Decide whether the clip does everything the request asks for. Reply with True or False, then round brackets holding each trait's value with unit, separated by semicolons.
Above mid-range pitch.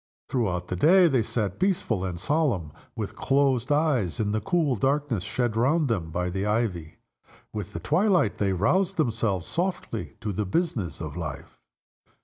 False (115 Hz)